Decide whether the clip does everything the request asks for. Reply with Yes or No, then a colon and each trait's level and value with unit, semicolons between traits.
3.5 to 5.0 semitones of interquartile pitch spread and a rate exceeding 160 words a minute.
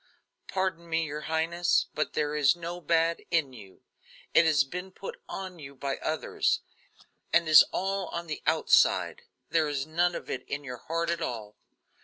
No: average, 2.9 semitones; average, 175 wpm